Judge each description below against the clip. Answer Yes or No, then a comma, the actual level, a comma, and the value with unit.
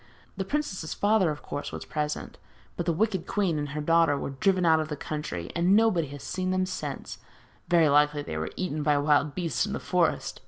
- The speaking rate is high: Yes, fast, 220 wpm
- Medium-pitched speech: Yes, medium, 160 Hz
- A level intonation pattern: No, average, 3.9 semitones